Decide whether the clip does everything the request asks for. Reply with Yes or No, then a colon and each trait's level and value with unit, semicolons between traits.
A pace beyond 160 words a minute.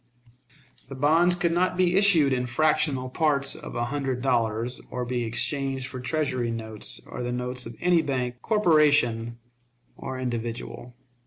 No: average, 150 wpm